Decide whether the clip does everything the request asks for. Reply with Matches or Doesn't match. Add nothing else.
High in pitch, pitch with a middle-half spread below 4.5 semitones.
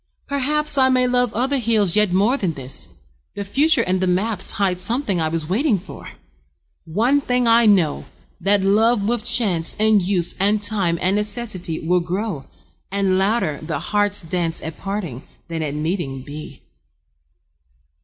Doesn't match